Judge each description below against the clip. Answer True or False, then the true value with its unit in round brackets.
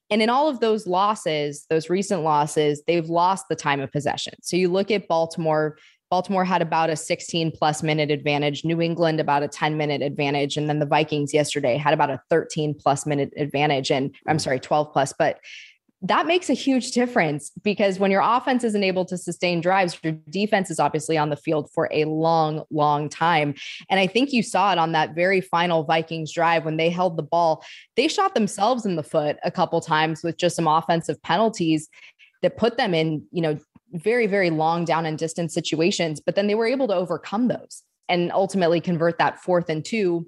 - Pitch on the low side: False (165 Hz)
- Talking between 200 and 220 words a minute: True (205 wpm)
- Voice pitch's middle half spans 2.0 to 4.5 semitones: True (3.4 semitones)